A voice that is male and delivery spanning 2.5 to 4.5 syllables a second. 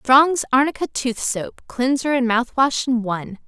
No: female; 4.3 syllables/s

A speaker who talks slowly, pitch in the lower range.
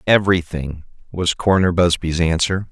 Yes: slow, 110 wpm; very low, 85 Hz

